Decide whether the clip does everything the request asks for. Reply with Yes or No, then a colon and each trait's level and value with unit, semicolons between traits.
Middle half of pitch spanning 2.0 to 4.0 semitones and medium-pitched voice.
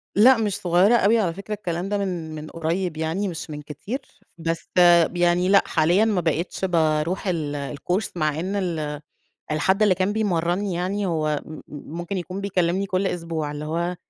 Yes: average, 3.6 semitones; medium, 175 Hz